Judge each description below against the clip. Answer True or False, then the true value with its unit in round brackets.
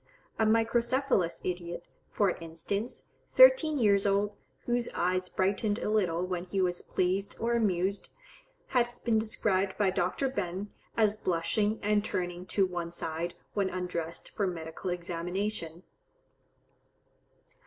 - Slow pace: True (125 wpm)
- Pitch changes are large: False (3.5 semitones)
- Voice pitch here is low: False (195 Hz)